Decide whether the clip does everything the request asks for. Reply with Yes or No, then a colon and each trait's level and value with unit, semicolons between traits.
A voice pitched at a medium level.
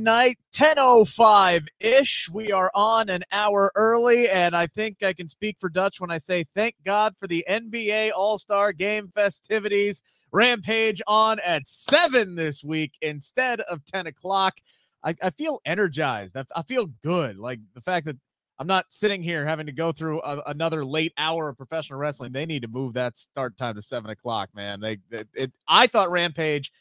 Yes: medium, 180 Hz